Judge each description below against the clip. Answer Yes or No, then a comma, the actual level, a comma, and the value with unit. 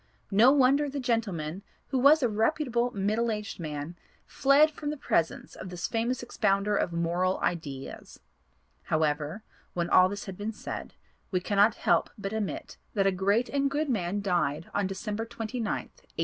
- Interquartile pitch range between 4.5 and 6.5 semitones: Yes, average, 5.2 semitones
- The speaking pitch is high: Yes, high, 205 Hz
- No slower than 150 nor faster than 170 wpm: Yes, average, 165 wpm